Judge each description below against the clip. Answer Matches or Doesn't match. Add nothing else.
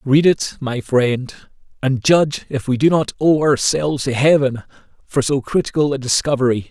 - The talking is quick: Doesn't match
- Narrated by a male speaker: Matches